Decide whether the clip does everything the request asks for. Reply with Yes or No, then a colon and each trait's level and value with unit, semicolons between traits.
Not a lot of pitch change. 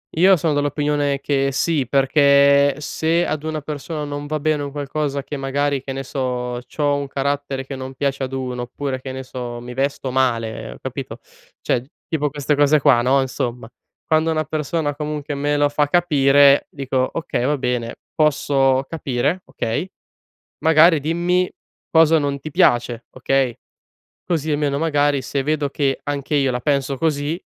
Yes: narrow, 2.2 semitones